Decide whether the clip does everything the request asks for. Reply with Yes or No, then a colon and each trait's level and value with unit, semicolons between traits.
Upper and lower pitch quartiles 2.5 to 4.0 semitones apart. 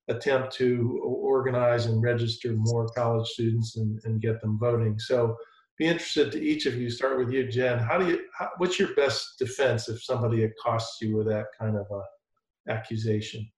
Yes: average, 2.9 semitones